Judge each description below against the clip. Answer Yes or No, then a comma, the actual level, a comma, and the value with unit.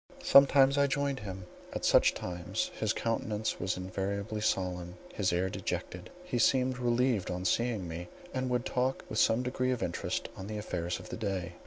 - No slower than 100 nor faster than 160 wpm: No, average, 180 wpm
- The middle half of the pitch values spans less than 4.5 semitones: No, wide, 5.5 semitones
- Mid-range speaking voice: No, low, 110 Hz